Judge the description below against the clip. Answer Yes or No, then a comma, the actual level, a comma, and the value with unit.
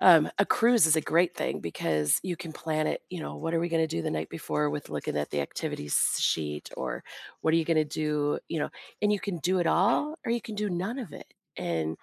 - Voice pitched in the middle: Yes, medium, 160 Hz